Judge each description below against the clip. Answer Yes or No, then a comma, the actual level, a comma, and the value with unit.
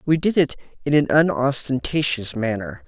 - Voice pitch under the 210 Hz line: Yes, low, 135 Hz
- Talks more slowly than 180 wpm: Yes, average, 145 wpm